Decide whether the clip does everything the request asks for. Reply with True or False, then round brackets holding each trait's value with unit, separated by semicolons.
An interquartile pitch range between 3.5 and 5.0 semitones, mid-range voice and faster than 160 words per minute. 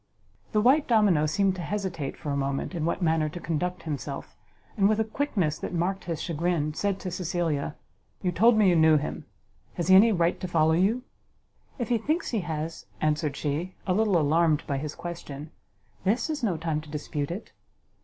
True (4.5 semitones; 170 Hz; 195 wpm)